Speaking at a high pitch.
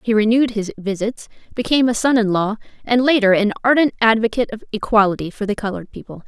Yes: high, 220 Hz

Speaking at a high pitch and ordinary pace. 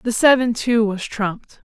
Yes: high, 225 Hz; average, 175 wpm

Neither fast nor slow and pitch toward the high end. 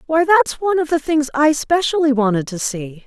No: fast, 215 wpm; very high, 285 Hz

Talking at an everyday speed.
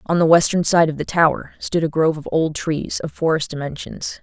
No: fast, 225 wpm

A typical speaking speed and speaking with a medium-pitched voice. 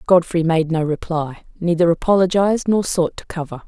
Yes: average, 145 wpm; medium, 170 Hz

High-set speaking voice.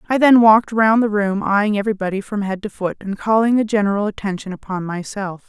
Yes: high, 205 Hz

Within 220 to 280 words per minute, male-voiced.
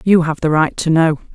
No: fast, 270 wpm; female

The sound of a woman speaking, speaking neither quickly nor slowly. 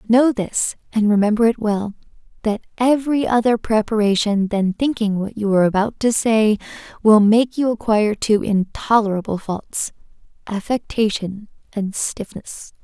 No: female; slow, 130 wpm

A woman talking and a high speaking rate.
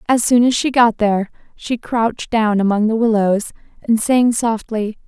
No: female; average, 175 wpm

